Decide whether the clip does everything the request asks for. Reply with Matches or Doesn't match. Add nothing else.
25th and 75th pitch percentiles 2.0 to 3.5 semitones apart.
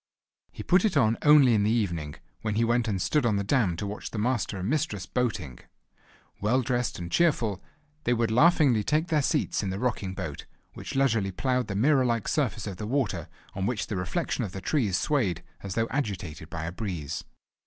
Doesn't match